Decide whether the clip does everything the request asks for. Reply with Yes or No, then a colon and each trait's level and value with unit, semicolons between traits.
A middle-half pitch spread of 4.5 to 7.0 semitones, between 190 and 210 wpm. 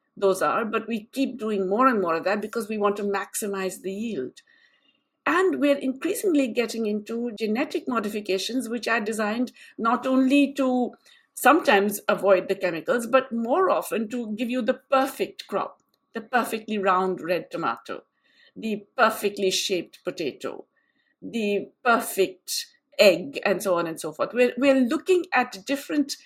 No: average, 4.8 semitones; average, 155 wpm